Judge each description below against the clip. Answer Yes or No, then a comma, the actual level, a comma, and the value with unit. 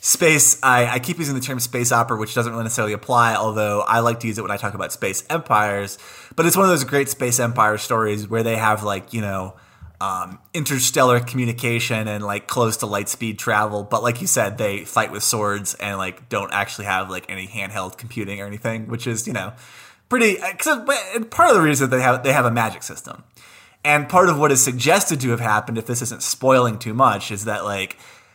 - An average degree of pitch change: Yes, average, 3.9 semitones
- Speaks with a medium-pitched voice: No, low, 115 Hz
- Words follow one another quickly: Yes, fast, 225 wpm